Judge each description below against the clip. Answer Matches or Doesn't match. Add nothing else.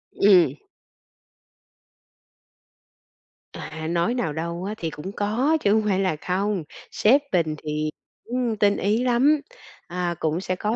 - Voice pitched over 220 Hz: Doesn't match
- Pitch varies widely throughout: Doesn't match